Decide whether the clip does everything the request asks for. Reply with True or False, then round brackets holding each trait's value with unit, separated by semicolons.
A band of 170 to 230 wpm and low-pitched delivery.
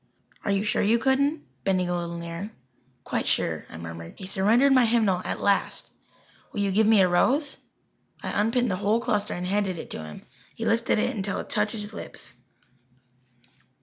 False (185 wpm; 205 Hz)